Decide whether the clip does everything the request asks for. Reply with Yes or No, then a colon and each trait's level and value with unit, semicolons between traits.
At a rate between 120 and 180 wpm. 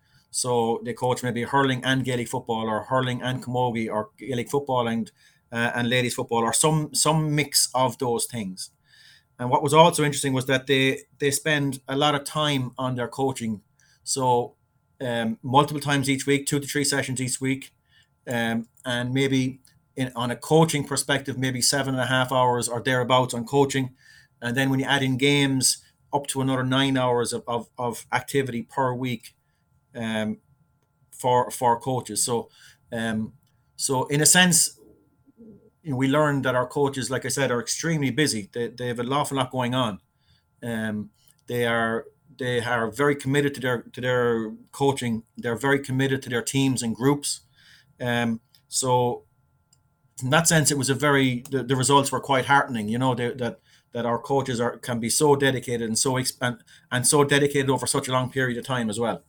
No: average, 190 wpm